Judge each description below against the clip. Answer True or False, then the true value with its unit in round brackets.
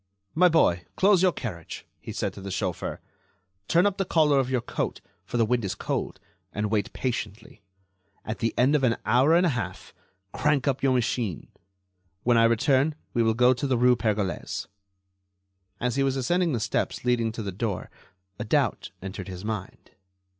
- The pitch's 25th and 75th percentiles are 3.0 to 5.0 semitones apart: True (4.2 semitones)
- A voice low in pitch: True (120 Hz)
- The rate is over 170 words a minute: True (185 wpm)